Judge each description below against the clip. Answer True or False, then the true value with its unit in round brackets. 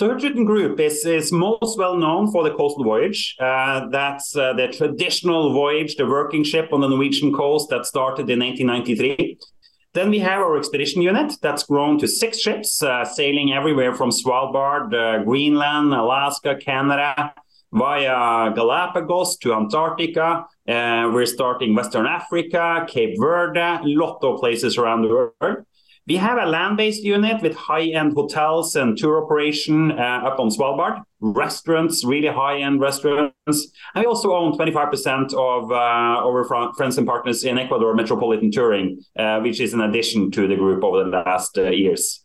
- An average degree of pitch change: True (4.6 semitones)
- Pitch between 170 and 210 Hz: False (145 Hz)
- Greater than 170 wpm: False (165 wpm)